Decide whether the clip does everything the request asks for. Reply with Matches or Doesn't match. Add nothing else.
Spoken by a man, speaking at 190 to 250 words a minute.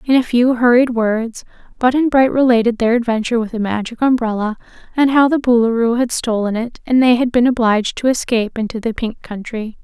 Doesn't match